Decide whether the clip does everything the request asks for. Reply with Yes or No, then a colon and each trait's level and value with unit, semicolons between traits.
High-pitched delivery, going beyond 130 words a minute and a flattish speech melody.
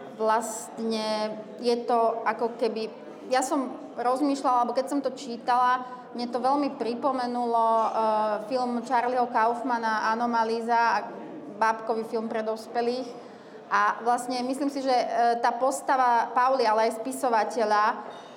No: high, 235 Hz; average, 125 wpm; narrow, 2.0 semitones